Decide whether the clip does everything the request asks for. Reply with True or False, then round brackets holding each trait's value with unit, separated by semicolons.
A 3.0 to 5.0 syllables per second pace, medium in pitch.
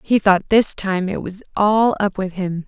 False (4.2 syllables/s; 195 Hz)